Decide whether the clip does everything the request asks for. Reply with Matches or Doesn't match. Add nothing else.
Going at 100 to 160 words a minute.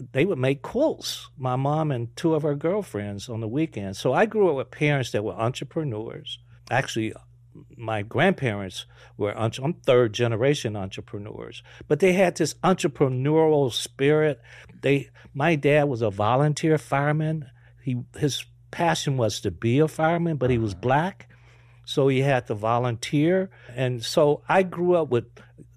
Matches